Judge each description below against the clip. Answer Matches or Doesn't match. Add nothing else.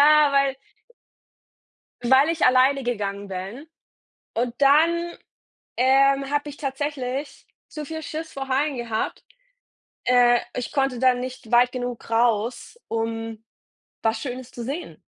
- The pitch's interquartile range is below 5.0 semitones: Matches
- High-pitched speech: Matches